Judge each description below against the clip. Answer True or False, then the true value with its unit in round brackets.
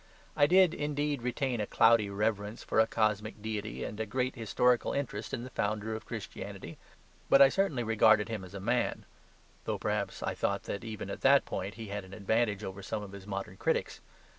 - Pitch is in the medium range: False (110 Hz)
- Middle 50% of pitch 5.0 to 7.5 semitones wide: False (3.2 semitones)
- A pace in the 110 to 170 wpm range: False (200 wpm)